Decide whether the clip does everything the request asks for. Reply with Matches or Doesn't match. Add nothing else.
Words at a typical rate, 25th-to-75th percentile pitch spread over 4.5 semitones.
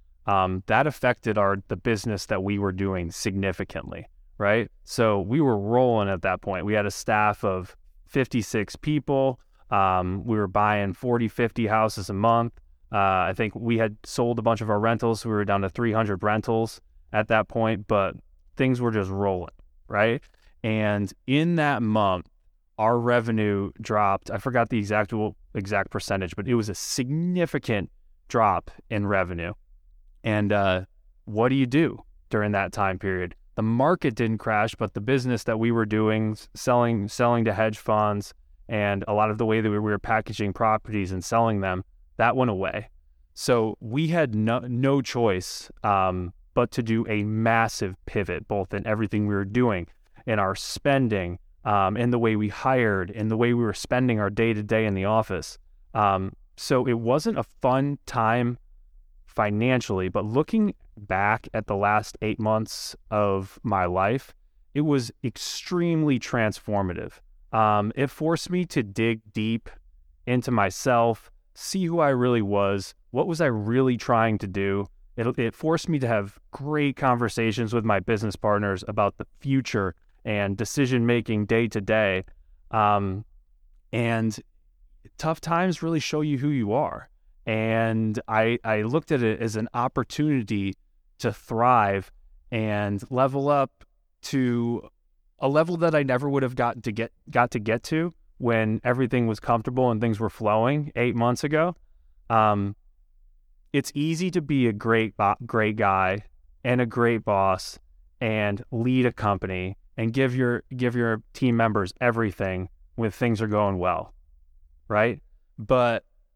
Doesn't match